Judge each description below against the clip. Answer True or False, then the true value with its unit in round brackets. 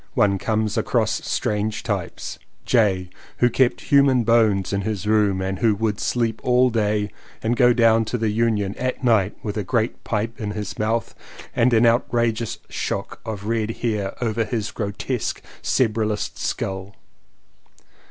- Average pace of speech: True (150 wpm)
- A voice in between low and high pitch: False (110 Hz)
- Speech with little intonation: True (2.2 semitones)